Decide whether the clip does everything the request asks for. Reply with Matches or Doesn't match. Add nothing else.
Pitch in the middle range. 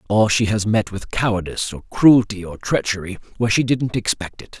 Doesn't match